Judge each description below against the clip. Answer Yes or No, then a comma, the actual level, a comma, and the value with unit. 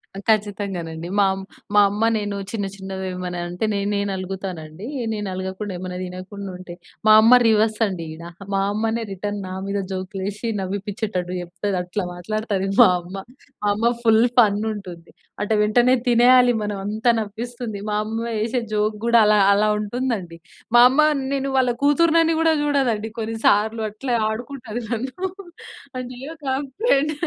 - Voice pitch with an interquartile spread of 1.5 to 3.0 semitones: No, average, 3.5 semitones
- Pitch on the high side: Yes, high, 210 Hz